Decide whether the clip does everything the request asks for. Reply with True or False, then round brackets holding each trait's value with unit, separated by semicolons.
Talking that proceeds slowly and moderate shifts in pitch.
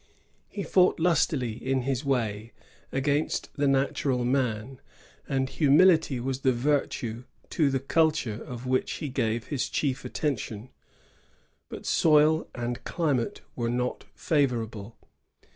True (125 wpm; 3.4 semitones)